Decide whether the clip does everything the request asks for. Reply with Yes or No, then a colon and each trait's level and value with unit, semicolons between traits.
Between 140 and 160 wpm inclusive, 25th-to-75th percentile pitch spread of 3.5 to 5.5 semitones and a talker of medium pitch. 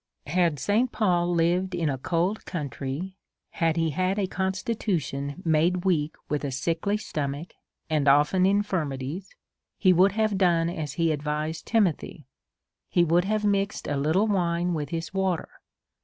Yes: average, 150 wpm; average, 3.9 semitones; medium, 175 Hz